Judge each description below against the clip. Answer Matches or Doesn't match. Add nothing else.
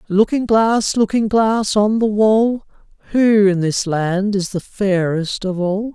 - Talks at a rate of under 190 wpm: Matches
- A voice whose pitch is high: Matches